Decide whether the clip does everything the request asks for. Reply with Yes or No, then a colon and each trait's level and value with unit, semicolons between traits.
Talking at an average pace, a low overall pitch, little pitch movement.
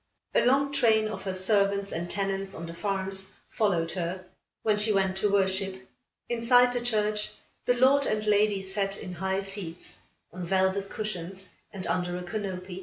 No: average, 170 wpm; high, 195 Hz; narrow, 2.1 semitones